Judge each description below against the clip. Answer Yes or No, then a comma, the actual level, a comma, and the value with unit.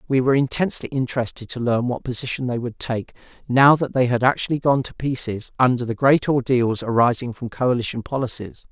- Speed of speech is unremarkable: Yes, average, 185 wpm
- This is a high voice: No, low, 125 Hz